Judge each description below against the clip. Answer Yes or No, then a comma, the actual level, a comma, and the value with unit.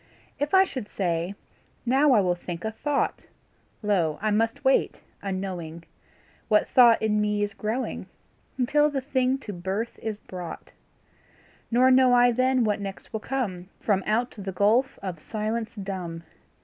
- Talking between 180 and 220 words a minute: No, average, 155 wpm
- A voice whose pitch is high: Yes, high, 215 Hz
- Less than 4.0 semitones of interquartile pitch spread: No, average, 4.7 semitones